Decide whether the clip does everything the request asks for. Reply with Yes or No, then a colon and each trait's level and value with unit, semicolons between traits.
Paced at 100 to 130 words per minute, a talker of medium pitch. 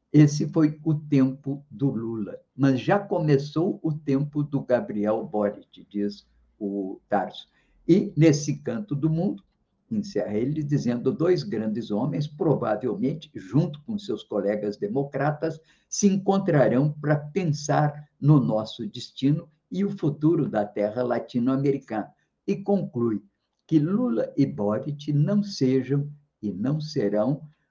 Yes: average, 125 wpm; medium, 145 Hz